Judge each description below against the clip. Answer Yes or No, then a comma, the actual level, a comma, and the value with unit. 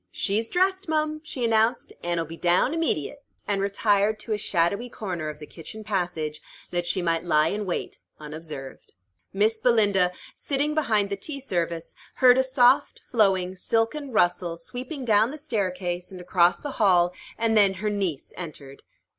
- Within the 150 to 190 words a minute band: Yes, average, 165 wpm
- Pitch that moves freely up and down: Yes, wide, 5.7 semitones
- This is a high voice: Yes, high, 200 Hz